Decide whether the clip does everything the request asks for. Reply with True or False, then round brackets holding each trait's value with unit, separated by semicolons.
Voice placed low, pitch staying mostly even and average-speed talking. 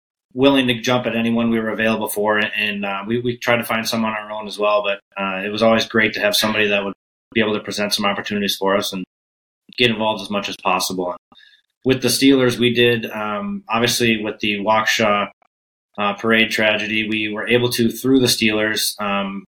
False (110 Hz; 2.3 semitones; 215 wpm)